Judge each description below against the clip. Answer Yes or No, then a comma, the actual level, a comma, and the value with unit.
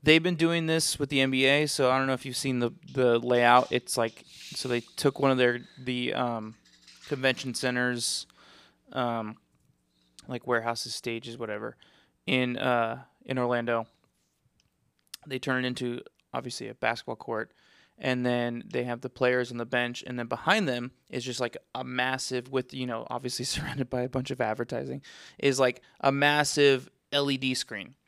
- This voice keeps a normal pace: Yes, average, 170 wpm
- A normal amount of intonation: No, narrow, 1.7 semitones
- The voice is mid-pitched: No, low, 125 Hz